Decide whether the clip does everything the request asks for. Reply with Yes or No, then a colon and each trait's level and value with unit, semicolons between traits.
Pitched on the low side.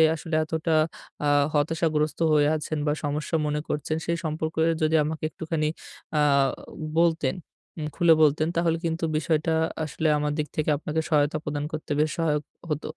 No: medium, 155 Hz